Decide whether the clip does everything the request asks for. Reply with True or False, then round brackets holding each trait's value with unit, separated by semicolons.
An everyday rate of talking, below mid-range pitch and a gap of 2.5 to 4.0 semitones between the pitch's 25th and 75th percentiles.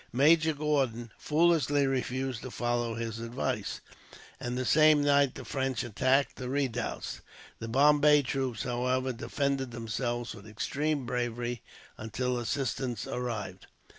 False (125 wpm; 125 Hz; 3.0 semitones)